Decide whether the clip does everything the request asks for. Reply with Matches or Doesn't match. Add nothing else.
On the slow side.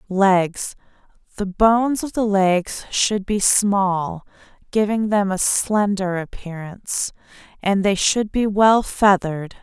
Matches